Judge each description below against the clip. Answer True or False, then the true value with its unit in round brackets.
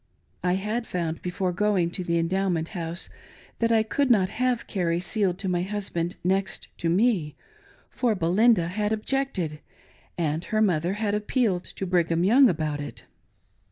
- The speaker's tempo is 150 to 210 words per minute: True (165 wpm)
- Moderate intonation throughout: True (4.0 semitones)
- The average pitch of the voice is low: False (185 Hz)